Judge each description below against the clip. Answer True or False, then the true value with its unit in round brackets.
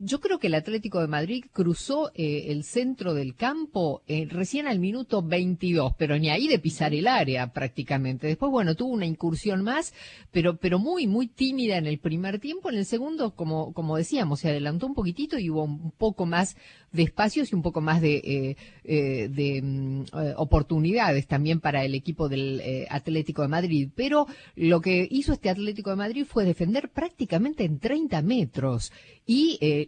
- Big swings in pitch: True (7.0 semitones)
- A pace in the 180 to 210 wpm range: True (185 wpm)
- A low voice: False (170 Hz)